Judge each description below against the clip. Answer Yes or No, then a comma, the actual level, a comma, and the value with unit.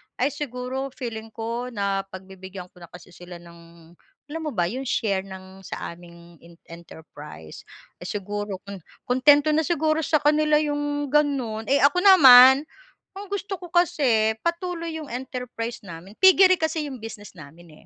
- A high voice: Yes, high, 245 Hz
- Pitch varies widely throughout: Yes, wide, 8.0 semitones